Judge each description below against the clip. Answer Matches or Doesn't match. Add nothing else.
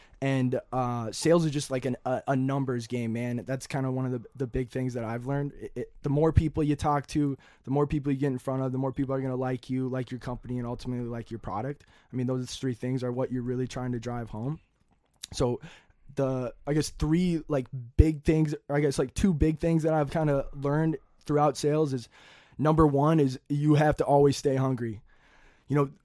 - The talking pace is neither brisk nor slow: Doesn't match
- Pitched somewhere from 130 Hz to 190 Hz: Matches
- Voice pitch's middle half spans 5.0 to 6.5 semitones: Doesn't match